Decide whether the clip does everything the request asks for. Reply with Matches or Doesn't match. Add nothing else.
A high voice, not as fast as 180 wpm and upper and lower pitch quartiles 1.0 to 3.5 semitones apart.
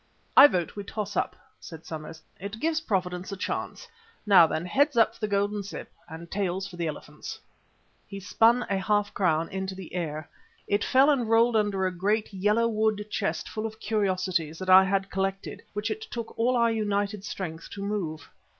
Doesn't match